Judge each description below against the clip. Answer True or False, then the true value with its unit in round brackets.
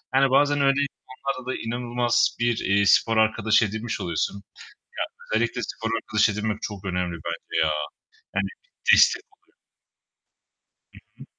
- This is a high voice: False (110 Hz)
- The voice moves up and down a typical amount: True (3.3 semitones)